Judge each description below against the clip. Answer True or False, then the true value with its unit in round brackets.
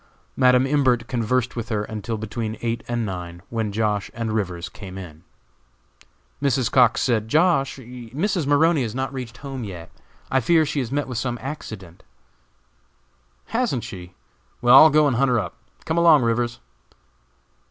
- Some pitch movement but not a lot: True (3.9 semitones)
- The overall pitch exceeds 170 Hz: False (120 Hz)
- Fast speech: False (160 wpm)